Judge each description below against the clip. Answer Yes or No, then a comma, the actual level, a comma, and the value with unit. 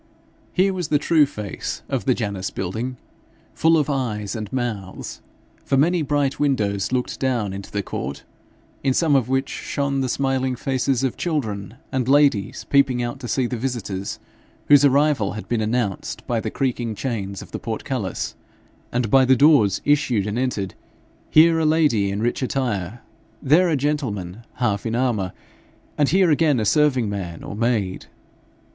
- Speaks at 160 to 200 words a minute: Yes, average, 165 wpm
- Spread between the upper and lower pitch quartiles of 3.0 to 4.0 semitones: No, average, 5.0 semitones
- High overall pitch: No, low, 125 Hz